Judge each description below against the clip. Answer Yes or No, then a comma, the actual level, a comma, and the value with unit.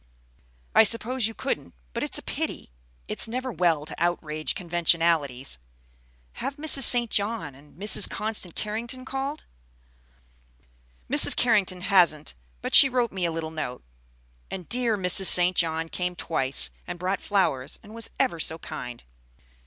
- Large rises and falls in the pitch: Yes, wide, 5.8 semitones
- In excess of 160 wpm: No, average, 145 wpm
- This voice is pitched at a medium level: Yes, medium, 180 Hz